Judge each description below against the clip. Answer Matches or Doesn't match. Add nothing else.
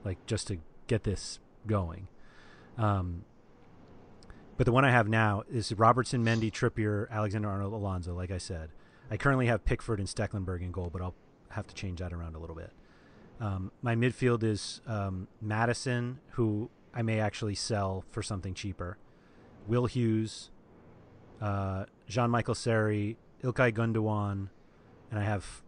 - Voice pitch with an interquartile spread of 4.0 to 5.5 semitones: Doesn't match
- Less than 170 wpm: Matches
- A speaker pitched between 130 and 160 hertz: Doesn't match